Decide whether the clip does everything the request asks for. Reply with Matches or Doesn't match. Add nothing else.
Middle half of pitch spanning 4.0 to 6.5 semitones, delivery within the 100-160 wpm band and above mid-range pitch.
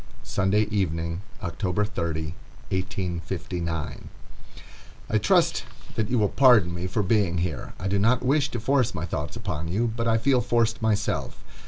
Doesn't match